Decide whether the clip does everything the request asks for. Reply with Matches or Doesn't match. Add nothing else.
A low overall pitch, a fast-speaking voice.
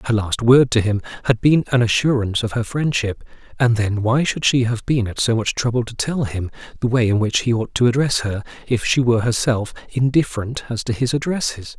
Matches